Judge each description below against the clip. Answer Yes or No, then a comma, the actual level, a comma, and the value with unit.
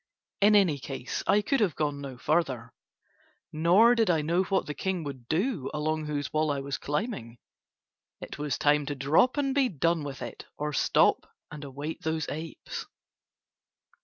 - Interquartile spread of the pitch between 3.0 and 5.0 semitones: Yes, average, 4.7 semitones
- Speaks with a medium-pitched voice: Yes, medium, 155 Hz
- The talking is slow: No, average, 170 wpm